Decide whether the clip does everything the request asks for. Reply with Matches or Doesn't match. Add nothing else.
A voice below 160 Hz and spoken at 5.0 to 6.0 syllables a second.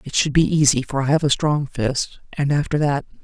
Matches